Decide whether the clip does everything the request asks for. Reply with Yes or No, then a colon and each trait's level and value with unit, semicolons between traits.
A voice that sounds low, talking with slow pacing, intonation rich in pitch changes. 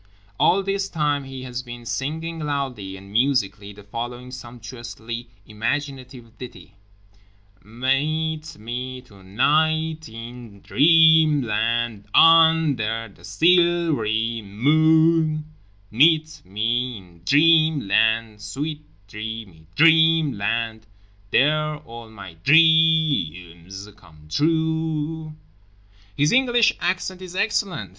Yes: low, 130 Hz; slow, 95 wpm; wide, 6.3 semitones